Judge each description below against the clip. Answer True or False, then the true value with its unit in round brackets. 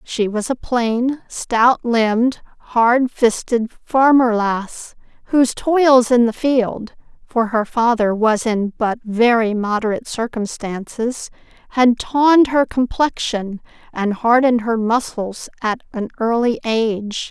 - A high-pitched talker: True (235 Hz)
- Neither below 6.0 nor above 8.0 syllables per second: False (3.8 syllables/s)